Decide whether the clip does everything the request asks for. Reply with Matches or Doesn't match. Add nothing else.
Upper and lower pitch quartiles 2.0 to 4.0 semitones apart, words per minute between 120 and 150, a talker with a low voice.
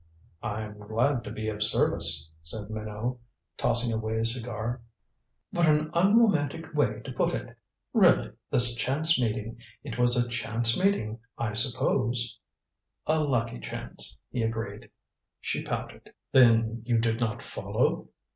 Matches